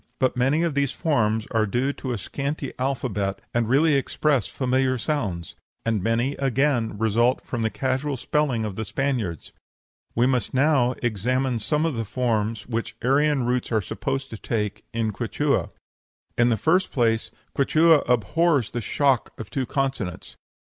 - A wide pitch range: No, average, 3.7 semitones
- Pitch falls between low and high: No, low, 125 Hz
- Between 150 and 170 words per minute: Yes, average, 160 wpm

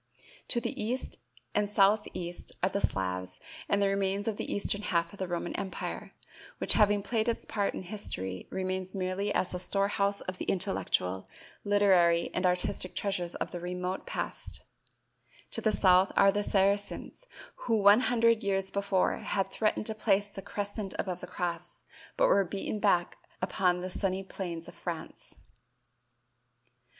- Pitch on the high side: Yes, high, 195 Hz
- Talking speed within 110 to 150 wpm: No, average, 160 wpm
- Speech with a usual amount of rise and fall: No, narrow, 2.2 semitones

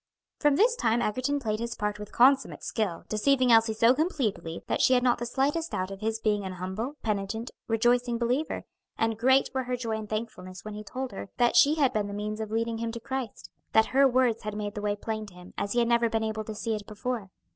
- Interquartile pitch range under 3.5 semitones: Yes, average, 2.9 semitones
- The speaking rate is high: Yes, fast, 245 wpm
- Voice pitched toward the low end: No, high, 225 Hz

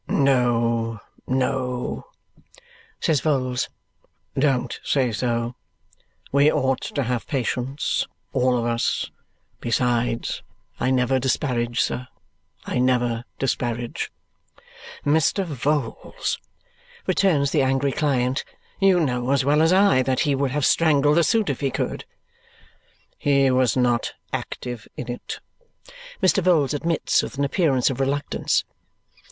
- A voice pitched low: Yes, low, 130 Hz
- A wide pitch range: No, average, 2.7 semitones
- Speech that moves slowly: Yes, slow, 120 wpm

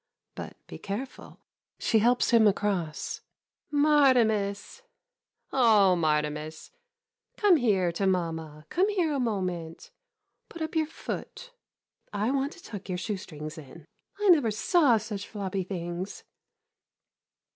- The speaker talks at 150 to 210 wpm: No, slow, 135 wpm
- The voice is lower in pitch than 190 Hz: No, high, 205 Hz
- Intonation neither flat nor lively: No, wide, 7.8 semitones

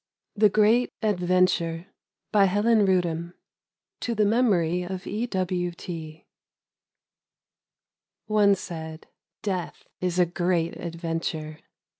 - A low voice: No, medium, 180 Hz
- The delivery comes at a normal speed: No, slow, 95 wpm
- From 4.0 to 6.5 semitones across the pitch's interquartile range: No, average, 3.5 semitones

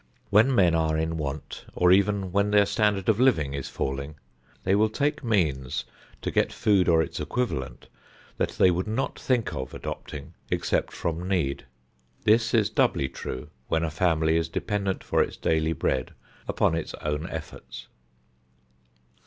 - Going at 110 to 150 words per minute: No, average, 160 wpm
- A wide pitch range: No, average, 4.9 semitones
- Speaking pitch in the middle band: No, very low, 85 Hz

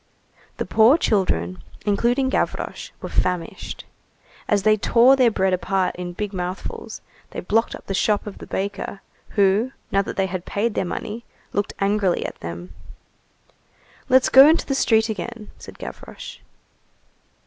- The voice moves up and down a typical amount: Yes, average, 3.5 semitones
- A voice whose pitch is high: Yes, high, 205 Hz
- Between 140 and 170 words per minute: Yes, average, 150 wpm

